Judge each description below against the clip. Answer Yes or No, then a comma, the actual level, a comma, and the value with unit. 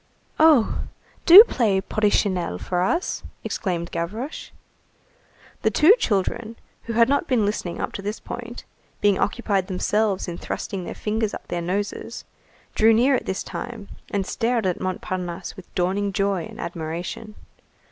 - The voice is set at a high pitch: Yes, high, 205 Hz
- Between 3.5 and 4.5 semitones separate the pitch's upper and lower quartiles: Yes, average, 3.9 semitones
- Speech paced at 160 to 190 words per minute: No, average, 145 wpm